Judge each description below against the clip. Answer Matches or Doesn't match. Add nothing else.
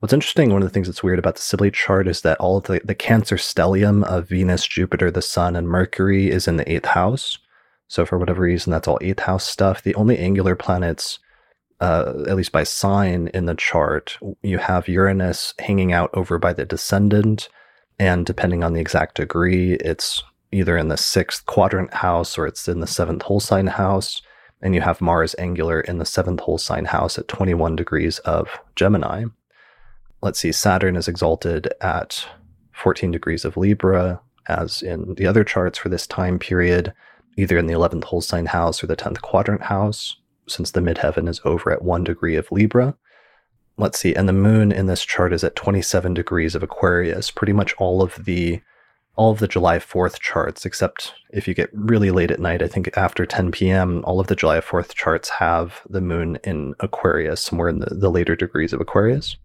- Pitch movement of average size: Doesn't match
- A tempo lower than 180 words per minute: Doesn't match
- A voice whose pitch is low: Matches